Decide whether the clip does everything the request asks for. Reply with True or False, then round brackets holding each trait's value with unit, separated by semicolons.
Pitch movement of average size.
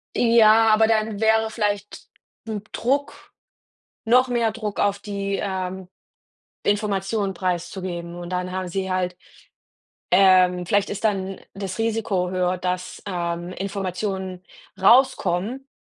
True (3.0 semitones)